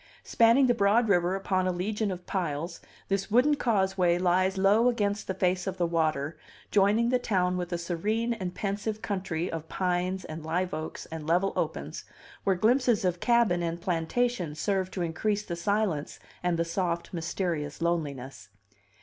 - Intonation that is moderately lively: Yes, average, 3.4 semitones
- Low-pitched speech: No, medium, 185 Hz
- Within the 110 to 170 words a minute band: Yes, average, 165 wpm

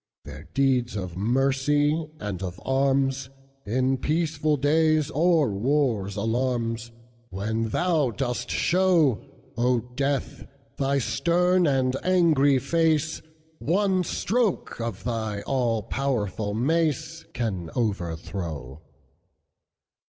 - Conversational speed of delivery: No, slow, 85 wpm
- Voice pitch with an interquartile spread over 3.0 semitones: Yes, wide, 5.4 semitones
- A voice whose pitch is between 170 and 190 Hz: No, low, 135 Hz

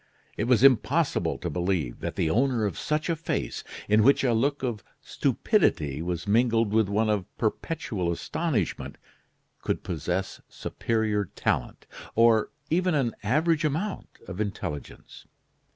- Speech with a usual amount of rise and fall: No, wide, 6.5 semitones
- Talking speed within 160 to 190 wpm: No, slow, 135 wpm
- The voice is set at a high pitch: No, low, 110 Hz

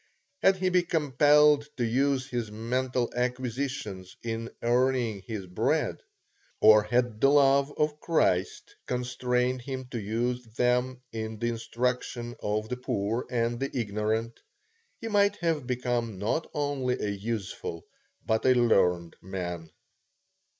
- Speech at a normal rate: No, slow, 130 wpm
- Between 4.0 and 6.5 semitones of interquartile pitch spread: No, average, 3.1 semitones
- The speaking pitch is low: Yes, low, 125 Hz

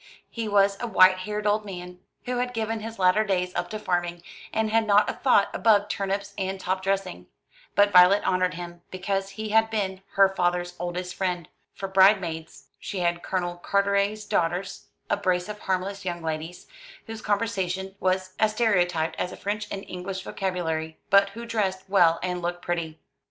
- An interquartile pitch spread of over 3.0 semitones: No, narrow, 2.4 semitones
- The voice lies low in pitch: No, high, 190 Hz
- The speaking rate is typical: Yes, average, 180 wpm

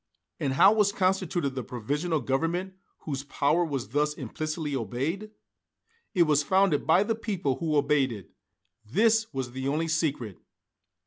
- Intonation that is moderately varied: Yes, average, 5.0 semitones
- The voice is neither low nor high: Yes, medium, 150 Hz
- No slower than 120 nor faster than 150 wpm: Yes, average, 145 wpm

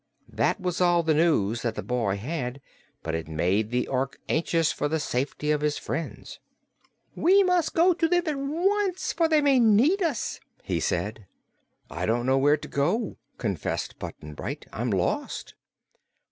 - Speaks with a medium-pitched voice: Yes, medium, 155 Hz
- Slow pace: No, average, 170 wpm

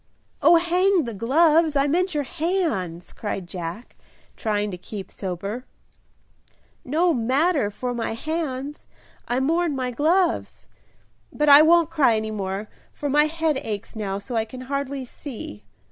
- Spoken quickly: No, average, 145 wpm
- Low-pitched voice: No, very high, 265 Hz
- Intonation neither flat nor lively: No, wide, 6.7 semitones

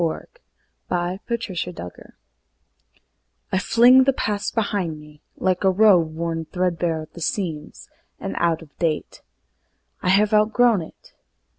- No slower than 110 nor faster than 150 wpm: Yes, average, 140 wpm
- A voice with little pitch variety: No, average, 4.3 semitones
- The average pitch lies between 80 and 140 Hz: No, medium, 180 Hz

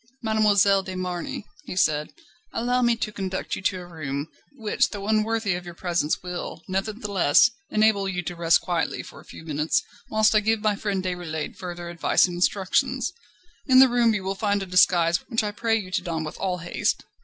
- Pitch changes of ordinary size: Yes, average, 3.6 semitones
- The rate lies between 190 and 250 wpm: Yes, average, 200 wpm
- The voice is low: No, high, 190 Hz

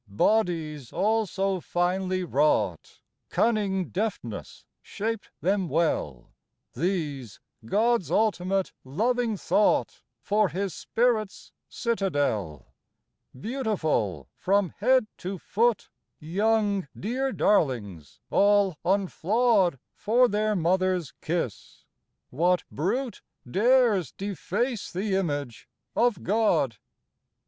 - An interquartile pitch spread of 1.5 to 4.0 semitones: No, wide, 5.4 semitones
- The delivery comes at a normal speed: No, slow, 90 wpm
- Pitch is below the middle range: No, high, 190 Hz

